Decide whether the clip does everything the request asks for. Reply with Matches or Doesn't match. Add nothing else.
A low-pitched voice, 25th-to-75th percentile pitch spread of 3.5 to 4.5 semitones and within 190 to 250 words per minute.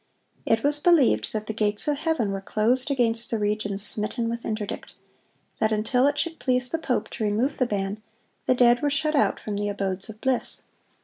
Doesn't match